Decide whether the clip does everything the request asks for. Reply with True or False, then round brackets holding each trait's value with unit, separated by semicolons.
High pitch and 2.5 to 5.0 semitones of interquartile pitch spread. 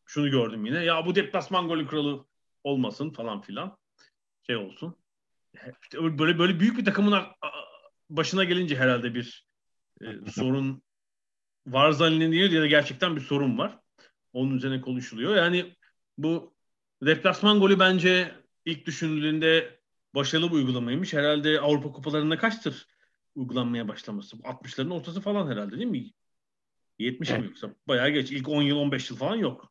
False (155 Hz; 4.6 semitones)